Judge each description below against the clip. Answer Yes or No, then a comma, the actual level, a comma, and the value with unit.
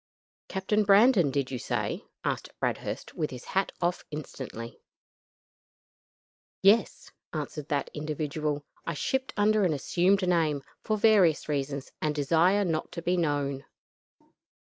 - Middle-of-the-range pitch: Yes, medium, 160 Hz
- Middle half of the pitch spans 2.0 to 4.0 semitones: No, average, 4.9 semitones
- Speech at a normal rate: No, slow, 125 wpm